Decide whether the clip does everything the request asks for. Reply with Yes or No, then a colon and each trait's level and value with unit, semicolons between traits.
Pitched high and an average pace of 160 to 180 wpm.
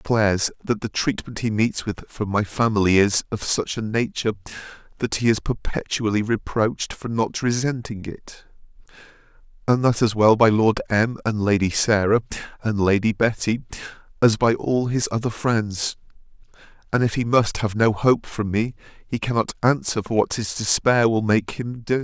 No: low, 110 Hz; average, 175 wpm